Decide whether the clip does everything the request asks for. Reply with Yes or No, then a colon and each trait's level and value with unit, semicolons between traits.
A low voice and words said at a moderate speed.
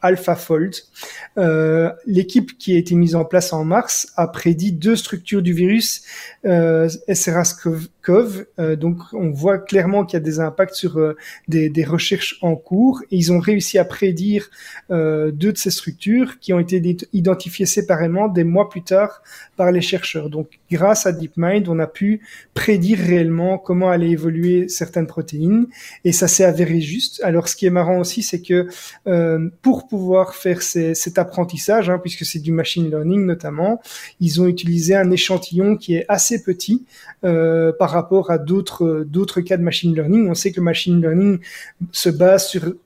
No: medium, 180 Hz; average, 180 wpm